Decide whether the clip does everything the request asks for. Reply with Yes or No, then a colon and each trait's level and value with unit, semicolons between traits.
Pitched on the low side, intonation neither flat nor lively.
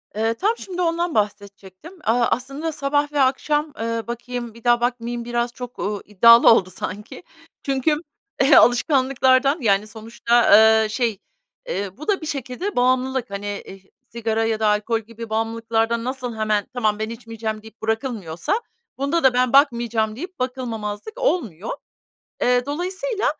No: high, 235 Hz; average, 3.7 semitones